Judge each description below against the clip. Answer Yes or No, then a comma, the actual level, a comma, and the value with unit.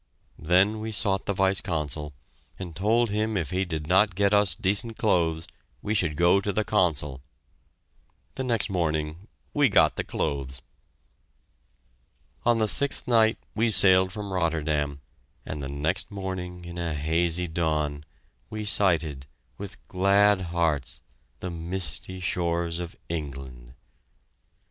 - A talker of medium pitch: No, very low, 90 Hz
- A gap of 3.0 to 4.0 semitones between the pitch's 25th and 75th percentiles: No, average, 4.5 semitones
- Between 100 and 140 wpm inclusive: Yes, slow, 135 wpm